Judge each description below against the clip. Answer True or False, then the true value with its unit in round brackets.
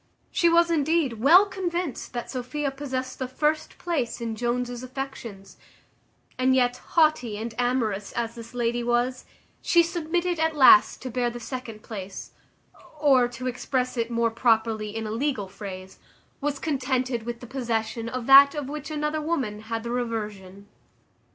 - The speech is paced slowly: False (155 wpm)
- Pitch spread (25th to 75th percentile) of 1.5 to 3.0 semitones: False (4.1 semitones)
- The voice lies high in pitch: True (250 Hz)